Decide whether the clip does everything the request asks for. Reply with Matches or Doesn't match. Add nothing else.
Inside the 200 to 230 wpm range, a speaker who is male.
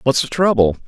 Matches